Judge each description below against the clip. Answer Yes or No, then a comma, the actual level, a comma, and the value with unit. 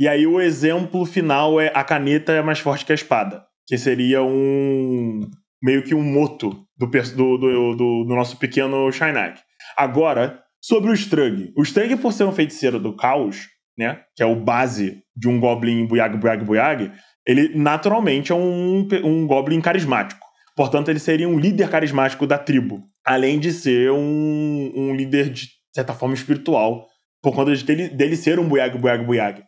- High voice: No, medium, 140 Hz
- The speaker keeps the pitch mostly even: No, average, 3.8 semitones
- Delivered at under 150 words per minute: No, average, 175 wpm